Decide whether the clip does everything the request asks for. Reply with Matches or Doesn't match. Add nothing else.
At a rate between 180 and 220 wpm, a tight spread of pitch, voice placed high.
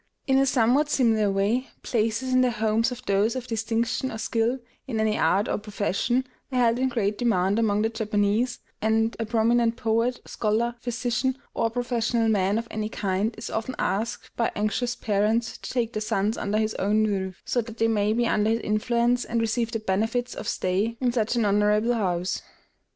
Matches